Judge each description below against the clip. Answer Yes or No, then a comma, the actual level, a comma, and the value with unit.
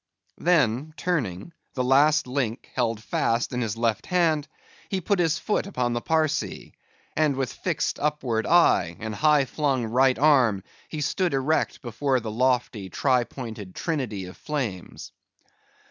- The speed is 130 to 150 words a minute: Yes, average, 145 wpm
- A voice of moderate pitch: No, low, 130 Hz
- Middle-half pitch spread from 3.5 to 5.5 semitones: Yes, average, 5.0 semitones